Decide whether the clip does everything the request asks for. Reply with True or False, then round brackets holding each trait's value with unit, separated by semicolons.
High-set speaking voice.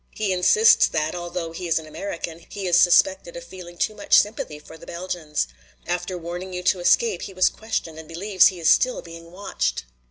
False (180 Hz)